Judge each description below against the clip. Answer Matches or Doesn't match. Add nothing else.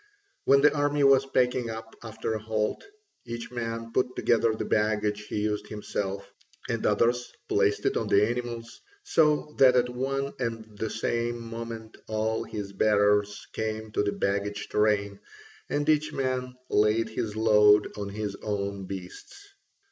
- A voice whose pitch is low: Matches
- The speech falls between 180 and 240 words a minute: Doesn't match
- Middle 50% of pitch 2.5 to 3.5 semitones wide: Matches